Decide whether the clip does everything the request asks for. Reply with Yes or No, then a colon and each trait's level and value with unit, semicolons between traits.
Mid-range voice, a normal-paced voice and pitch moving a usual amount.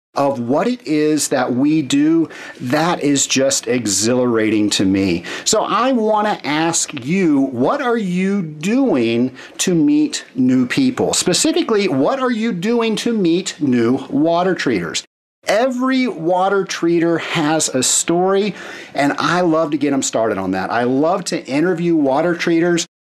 No: medium, 175 Hz; average, 150 wpm; wide, 8.5 semitones